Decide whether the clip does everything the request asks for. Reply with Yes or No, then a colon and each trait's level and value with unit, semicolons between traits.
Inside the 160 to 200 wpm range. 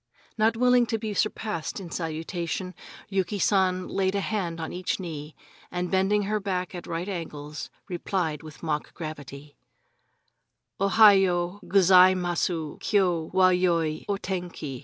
No: slow, 135 wpm